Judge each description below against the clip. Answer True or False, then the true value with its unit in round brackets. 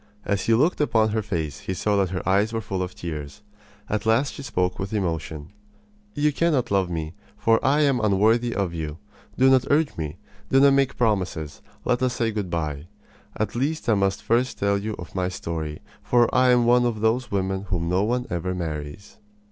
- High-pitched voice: False (105 Hz)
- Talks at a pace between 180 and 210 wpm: True (205 wpm)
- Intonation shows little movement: False (5.4 semitones)